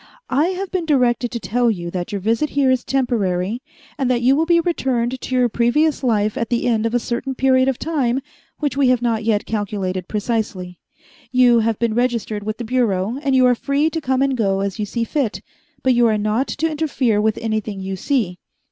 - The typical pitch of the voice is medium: No, high, 240 Hz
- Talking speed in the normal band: No, fast, 220 wpm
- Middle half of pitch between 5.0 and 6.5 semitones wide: No, average, 3.7 semitones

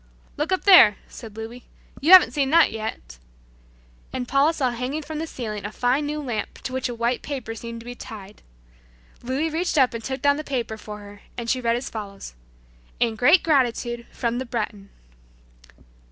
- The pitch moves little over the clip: No, average, 4.2 semitones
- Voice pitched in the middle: No, high, 245 Hz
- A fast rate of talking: No, average, 190 wpm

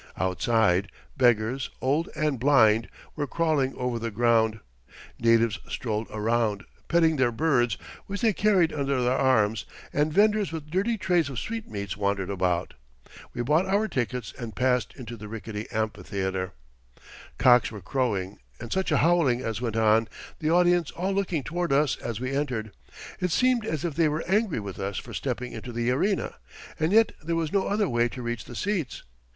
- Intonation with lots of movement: Yes, wide, 6.8 semitones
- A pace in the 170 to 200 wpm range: Yes, average, 175 wpm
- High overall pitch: No, low, 125 Hz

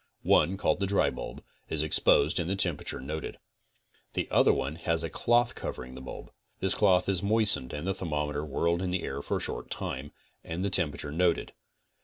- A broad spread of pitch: No, average, 4.5 semitones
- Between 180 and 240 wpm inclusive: Yes, average, 200 wpm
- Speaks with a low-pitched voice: Yes, very low, 85 Hz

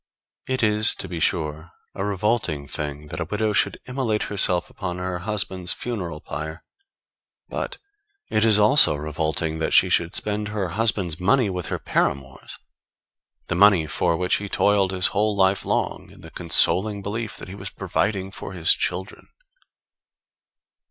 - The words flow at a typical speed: Yes, average, 160 wpm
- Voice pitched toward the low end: Yes, very low, 95 Hz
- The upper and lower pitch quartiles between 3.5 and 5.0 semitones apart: Yes, average, 3.9 semitones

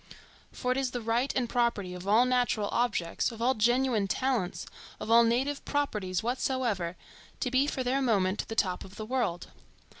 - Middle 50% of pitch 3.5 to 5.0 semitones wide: Yes, average, 3.9 semitones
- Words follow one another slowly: No, average, 180 wpm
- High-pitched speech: Yes, high, 235 Hz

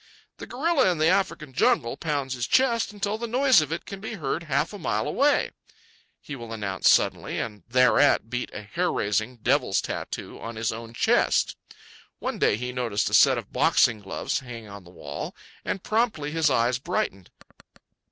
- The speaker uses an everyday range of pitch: No, wide, 9.0 semitones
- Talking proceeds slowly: No, average, 180 wpm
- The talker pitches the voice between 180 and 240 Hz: No, low, 130 Hz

